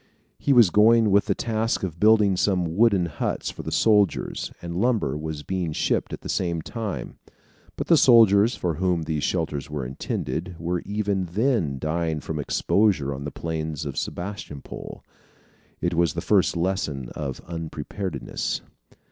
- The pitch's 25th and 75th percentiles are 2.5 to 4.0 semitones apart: No, average, 4.8 semitones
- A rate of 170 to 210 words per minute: No, average, 155 wpm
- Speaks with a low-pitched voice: Yes, very low, 90 Hz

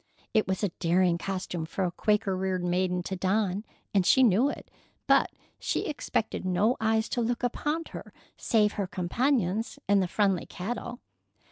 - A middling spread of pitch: Yes, average, 3.5 semitones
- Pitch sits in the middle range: No, high, 195 Hz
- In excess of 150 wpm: Yes, average, 165 wpm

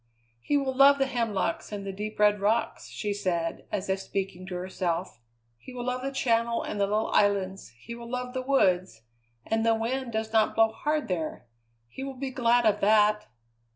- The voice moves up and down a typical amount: Yes, average, 4.4 semitones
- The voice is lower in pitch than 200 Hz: No, high, 220 Hz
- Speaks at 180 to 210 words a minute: Yes, average, 195 wpm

